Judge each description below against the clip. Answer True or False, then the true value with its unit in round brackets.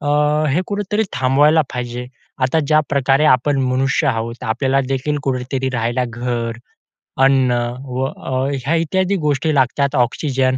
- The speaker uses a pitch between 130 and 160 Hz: True (135 Hz)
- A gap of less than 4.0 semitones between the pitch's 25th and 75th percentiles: True (2.7 semitones)